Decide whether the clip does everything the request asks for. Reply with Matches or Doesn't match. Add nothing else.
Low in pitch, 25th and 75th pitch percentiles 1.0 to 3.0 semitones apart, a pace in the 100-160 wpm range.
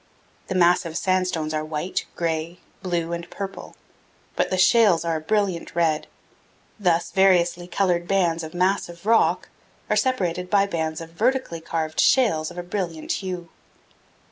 Doesn't match